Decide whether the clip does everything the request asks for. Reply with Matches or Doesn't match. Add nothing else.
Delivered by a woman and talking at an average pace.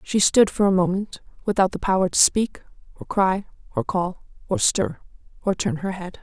Matches